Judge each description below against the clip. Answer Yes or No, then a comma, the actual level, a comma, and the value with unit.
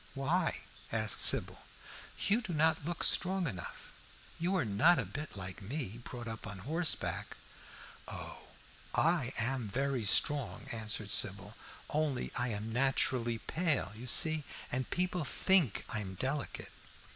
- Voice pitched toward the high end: No, low, 130 Hz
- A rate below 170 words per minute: Yes, average, 140 wpm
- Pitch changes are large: Yes, wide, 6.3 semitones